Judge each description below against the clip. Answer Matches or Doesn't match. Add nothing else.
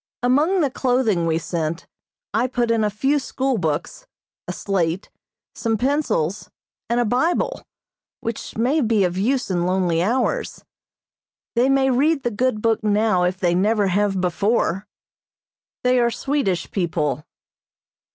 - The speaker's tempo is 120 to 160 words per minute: Matches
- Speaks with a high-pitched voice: Matches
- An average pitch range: Doesn't match